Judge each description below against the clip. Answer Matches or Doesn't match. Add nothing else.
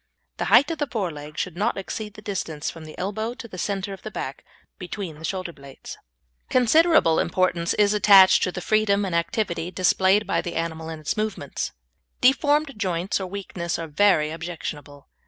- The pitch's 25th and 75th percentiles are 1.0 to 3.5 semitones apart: Doesn't match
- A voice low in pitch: Doesn't match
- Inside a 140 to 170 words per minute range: Doesn't match